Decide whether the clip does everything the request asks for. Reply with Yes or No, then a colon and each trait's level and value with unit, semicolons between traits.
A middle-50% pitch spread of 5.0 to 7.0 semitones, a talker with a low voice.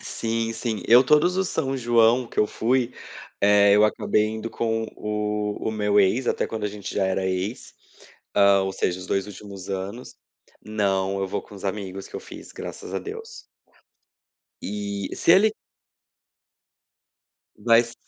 No: average, 2.9 semitones; low, 105 Hz